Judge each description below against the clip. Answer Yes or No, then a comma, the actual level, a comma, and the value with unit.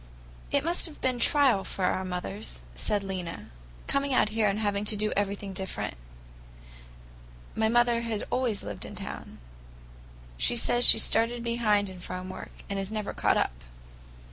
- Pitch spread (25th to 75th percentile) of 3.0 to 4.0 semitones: Yes, average, 3.6 semitones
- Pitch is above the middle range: Yes, high, 210 Hz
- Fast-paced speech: No, average, 170 wpm